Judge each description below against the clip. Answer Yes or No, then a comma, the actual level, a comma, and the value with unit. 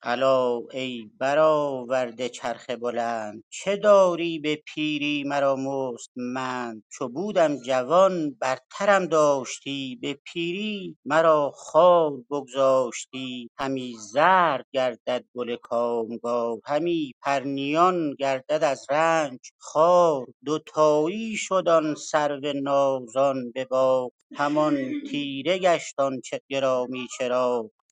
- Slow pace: Yes, slow, 100 wpm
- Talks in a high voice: No, medium, 140 Hz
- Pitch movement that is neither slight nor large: Yes, average, 3.8 semitones